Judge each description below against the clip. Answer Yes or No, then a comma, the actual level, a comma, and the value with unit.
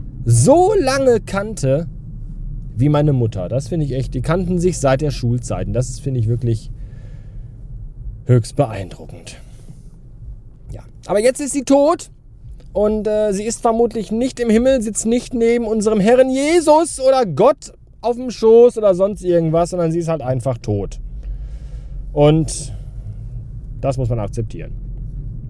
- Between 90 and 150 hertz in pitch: Yes, medium, 140 Hz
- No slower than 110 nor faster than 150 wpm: Yes, average, 145 wpm